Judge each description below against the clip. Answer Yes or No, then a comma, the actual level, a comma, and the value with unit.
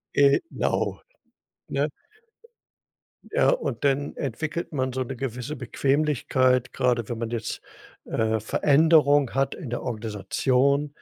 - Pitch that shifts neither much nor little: Yes, average, 3.1 semitones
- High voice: No, low, 135 Hz